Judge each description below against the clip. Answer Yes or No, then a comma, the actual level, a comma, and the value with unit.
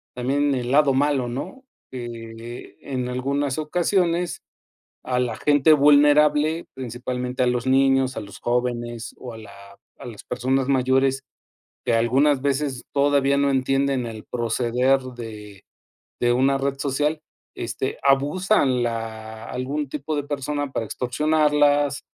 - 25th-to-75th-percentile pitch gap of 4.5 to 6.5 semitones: No, average, 2.9 semitones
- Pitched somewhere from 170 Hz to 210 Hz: No, low, 135 Hz